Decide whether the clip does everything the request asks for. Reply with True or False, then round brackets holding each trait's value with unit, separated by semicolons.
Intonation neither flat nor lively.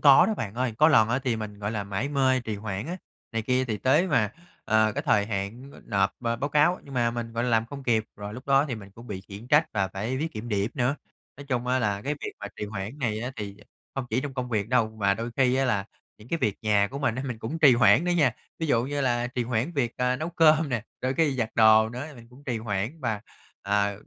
True (4.0 semitones)